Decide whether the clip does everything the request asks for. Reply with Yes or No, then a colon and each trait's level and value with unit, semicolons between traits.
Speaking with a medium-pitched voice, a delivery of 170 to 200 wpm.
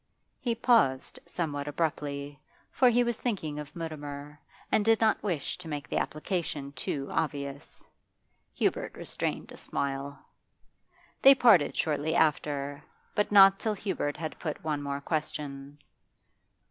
No: medium, 150 Hz; slow, 135 wpm